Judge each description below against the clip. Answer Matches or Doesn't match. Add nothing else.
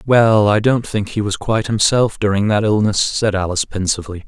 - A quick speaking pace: Doesn't match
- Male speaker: Matches